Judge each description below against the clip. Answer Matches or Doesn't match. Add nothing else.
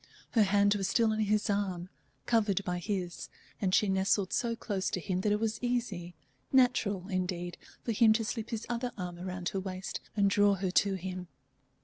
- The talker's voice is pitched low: Doesn't match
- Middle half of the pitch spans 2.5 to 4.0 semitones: Matches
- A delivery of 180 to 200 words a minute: Matches